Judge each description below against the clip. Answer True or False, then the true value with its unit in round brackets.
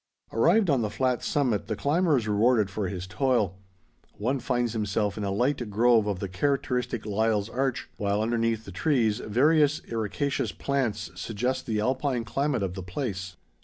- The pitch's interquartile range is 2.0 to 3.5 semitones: False (4.2 semitones)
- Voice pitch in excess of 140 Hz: False (115 Hz)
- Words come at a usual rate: True (165 wpm)